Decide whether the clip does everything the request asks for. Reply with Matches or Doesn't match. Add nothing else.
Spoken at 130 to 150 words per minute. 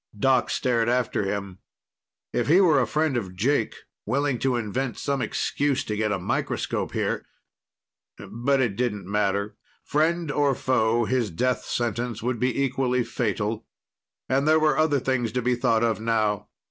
Doesn't match